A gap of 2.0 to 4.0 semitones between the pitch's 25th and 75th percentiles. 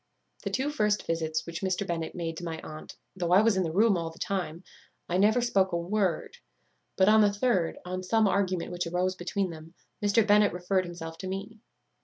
Yes: average, 3.2 semitones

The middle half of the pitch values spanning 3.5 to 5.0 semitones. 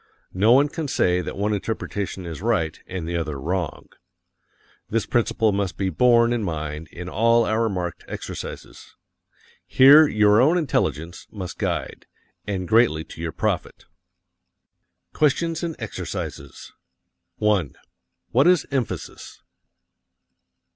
No: wide, 5.4 semitones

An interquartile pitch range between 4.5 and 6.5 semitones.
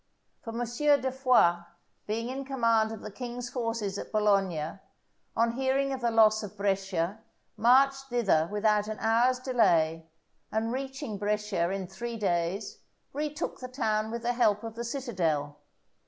No: average, 3.8 semitones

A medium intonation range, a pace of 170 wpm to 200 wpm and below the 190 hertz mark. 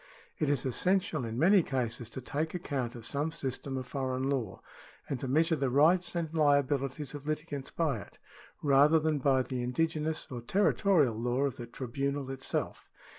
Yes: average, 3.5 semitones; average, 175 wpm; medium, 140 Hz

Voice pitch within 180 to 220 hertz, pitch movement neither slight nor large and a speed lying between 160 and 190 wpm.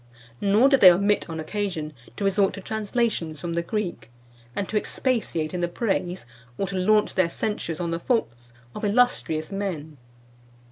Yes: high, 190 Hz; average, 4.0 semitones; average, 170 wpm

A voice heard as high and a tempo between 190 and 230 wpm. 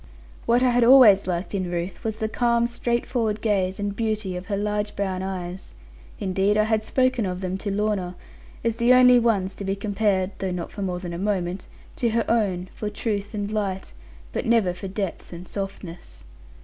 Yes: high, 205 Hz; average, 195 wpm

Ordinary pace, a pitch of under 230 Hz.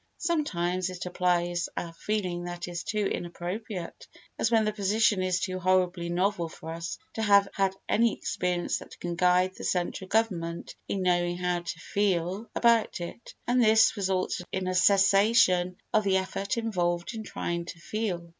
Yes: average, 165 wpm; medium, 185 Hz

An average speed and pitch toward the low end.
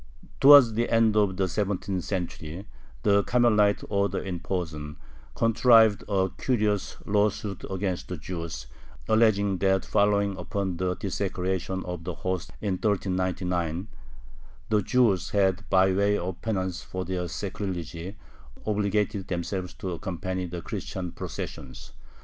No: slow, 125 wpm; very low, 95 Hz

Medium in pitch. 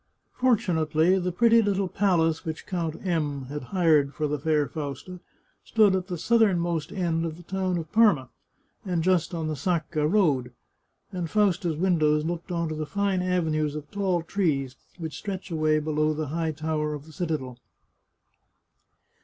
Yes: medium, 165 Hz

